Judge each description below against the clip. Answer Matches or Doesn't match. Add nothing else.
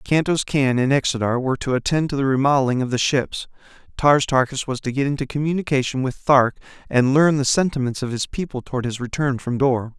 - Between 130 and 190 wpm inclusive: Doesn't match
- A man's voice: Matches